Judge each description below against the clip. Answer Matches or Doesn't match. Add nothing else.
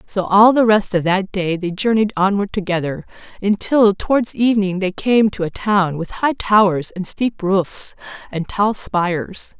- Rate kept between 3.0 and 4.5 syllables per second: Matches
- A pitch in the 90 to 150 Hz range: Doesn't match